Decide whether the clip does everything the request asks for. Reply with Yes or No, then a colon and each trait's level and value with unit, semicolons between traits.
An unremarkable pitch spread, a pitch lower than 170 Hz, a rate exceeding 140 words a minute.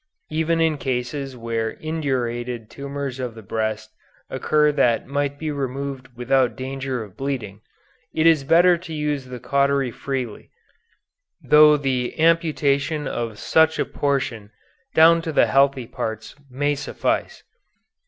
No: average, 3.5 semitones; low, 135 Hz; slow, 135 wpm